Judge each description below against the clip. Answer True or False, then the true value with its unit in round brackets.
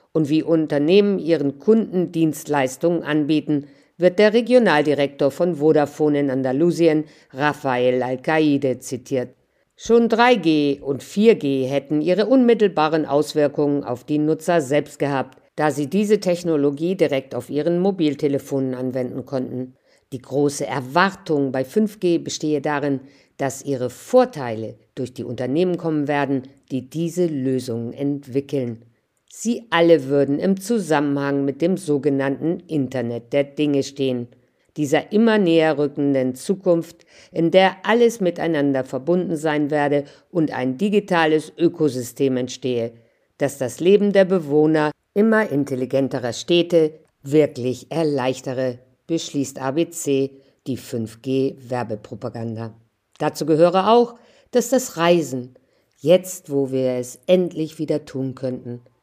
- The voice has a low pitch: False (145 Hz)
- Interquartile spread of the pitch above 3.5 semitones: True (4.1 semitones)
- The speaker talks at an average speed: False (120 wpm)